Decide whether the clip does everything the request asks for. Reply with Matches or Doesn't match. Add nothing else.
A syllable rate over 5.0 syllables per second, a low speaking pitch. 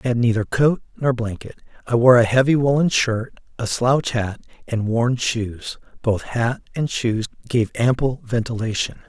Doesn't match